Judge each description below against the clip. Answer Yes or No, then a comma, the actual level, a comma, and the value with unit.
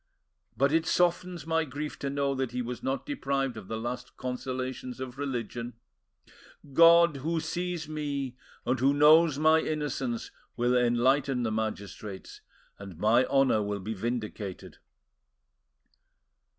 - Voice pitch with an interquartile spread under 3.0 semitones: No, average, 4.1 semitones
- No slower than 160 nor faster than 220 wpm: No, slow, 135 wpm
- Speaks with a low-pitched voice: Yes, low, 130 Hz